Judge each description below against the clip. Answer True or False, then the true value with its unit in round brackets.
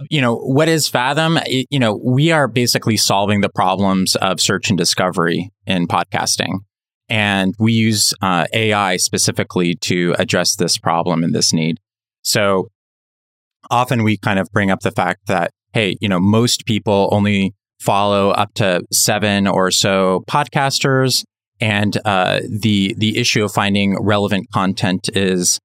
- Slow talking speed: False (155 wpm)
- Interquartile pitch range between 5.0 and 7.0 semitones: False (3.6 semitones)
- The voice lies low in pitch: True (105 Hz)